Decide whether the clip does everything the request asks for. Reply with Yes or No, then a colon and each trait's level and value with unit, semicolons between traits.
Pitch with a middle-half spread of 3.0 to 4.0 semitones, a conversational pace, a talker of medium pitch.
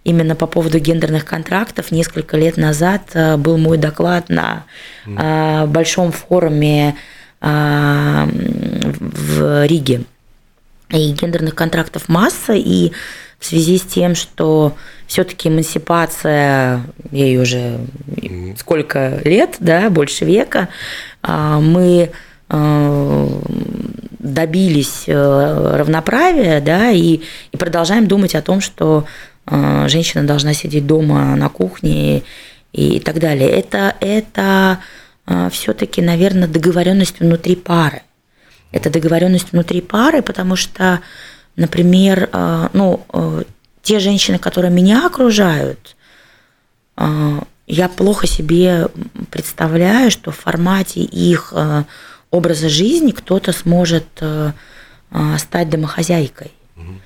No: average, 3.7 semitones; slow, 95 wpm; medium, 160 Hz